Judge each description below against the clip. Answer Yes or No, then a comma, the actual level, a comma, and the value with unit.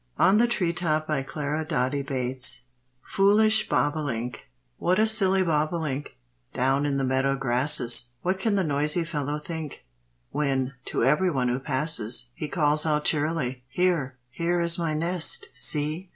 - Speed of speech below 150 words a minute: Yes, slow, 135 wpm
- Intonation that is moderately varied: Yes, average, 4.0 semitones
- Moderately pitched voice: Yes, medium, 150 Hz